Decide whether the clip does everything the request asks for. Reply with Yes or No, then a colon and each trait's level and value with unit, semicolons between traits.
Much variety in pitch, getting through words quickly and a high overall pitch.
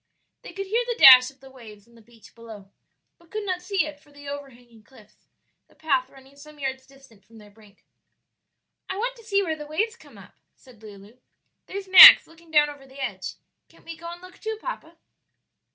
Yes: wide, 6.5 semitones; fast, 215 wpm; very high, 280 Hz